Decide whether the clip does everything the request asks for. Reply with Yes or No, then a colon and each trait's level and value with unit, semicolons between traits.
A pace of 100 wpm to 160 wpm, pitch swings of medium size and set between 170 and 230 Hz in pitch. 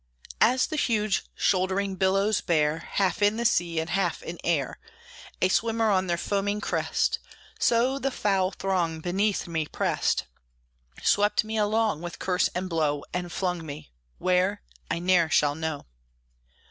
Yes: average, 150 wpm; average, 3.6 semitones; medium, 185 Hz